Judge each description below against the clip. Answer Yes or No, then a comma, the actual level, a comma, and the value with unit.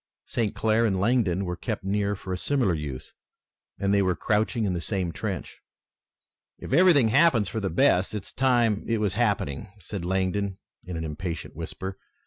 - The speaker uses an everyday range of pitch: Yes, average, 3.5 semitones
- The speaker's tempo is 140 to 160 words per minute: No, average, 175 wpm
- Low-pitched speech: Yes, low, 100 Hz